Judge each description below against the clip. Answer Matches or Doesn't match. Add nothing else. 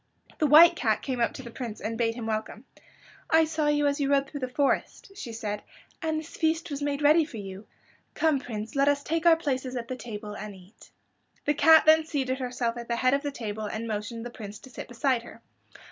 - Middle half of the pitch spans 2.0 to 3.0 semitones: Doesn't match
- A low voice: Doesn't match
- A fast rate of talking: Matches